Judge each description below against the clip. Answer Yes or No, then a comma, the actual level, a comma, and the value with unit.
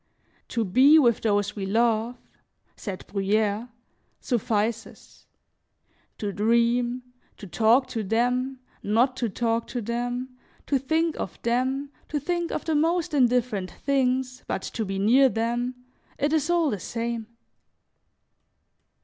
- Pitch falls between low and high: No, high, 240 Hz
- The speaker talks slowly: Yes, slow, 130 wpm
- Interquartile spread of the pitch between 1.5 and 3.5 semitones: Yes, average, 3.0 semitones